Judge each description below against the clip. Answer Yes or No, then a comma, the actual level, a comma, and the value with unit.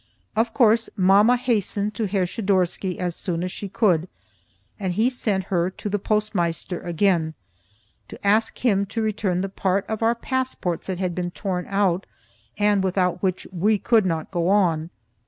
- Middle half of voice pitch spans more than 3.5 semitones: No, average, 3.0 semitones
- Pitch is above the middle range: Yes, high, 195 Hz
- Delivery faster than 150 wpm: Yes, average, 170 wpm